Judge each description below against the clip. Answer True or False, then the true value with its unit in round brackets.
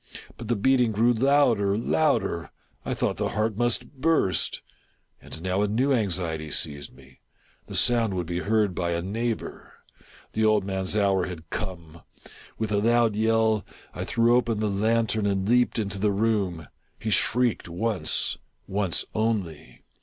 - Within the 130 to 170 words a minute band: True (160 wpm)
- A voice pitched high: False (105 Hz)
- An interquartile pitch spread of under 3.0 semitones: False (3.7 semitones)